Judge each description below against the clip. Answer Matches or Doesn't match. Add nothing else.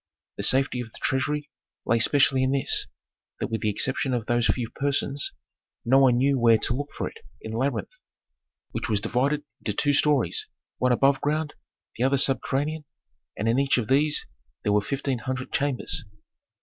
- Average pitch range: Matches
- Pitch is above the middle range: Doesn't match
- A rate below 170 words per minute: Doesn't match